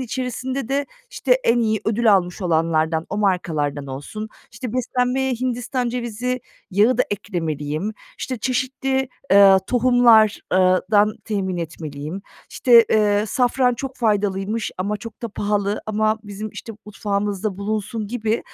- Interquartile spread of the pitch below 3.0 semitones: No, average, 4.2 semitones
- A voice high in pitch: Yes, high, 215 Hz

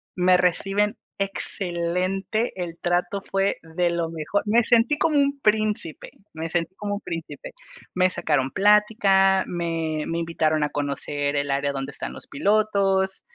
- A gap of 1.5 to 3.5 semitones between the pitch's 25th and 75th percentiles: No, average, 3.9 semitones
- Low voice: No, medium, 180 Hz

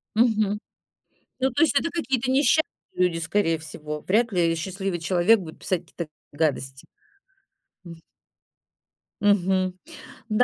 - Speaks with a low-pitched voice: No, medium, 185 Hz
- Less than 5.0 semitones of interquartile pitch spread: No, average, 5.3 semitones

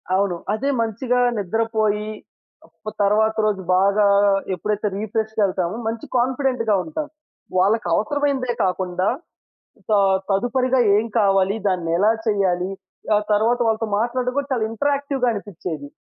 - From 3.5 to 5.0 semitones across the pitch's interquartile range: Yes, average, 3.9 semitones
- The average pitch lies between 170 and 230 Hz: Yes, high, 215 Hz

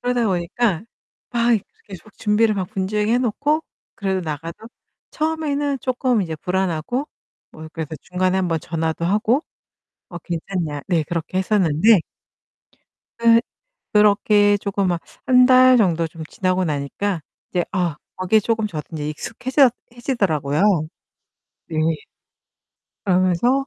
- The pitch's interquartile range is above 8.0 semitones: No, wide, 5.6 semitones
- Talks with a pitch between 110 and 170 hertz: No, high, 195 Hz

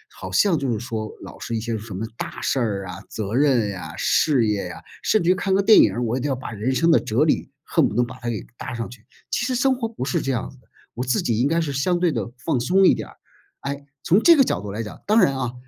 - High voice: No, low, 125 Hz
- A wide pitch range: Yes, wide, 6.5 semitones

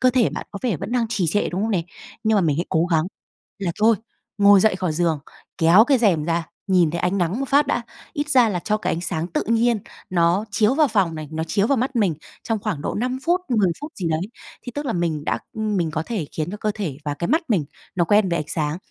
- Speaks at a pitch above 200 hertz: No, high, 195 Hz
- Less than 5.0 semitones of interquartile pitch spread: No, average, 5.3 semitones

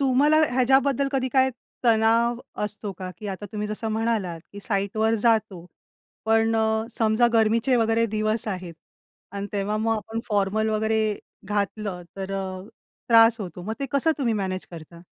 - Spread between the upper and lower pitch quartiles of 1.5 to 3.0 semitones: Yes, narrow, 2.4 semitones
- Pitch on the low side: No, high, 220 Hz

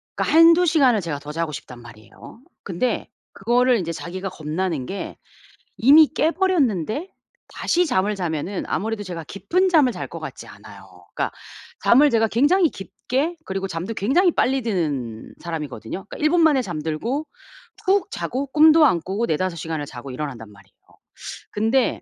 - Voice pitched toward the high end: Yes, high, 205 Hz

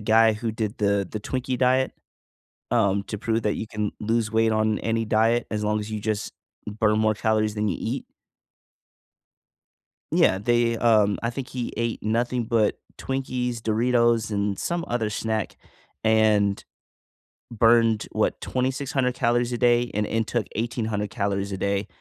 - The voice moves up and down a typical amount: No, narrow, 2.1 semitones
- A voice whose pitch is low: Yes, low, 110 Hz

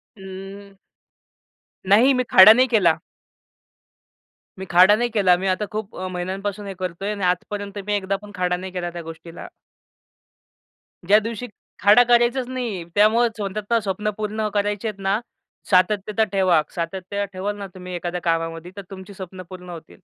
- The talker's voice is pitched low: No, high, 195 Hz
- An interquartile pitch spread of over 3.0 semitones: No, narrow, 2.6 semitones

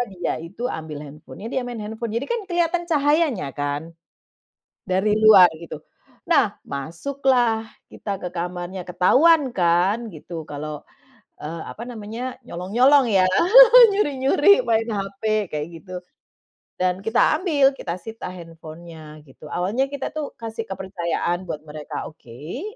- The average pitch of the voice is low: No, high, 195 Hz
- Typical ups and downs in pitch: No, wide, 6.9 semitones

